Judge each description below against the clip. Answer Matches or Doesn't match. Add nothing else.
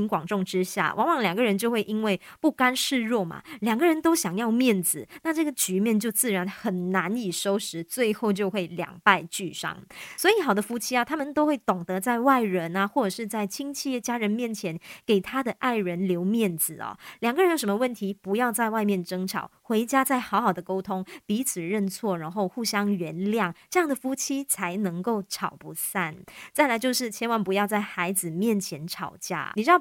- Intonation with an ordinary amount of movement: Matches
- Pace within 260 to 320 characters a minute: Matches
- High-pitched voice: Matches